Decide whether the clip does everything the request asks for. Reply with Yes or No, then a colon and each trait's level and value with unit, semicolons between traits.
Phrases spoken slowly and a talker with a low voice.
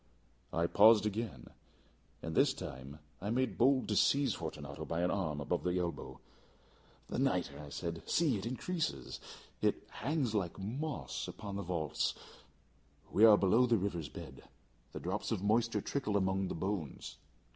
No: average, 155 wpm; low, 100 Hz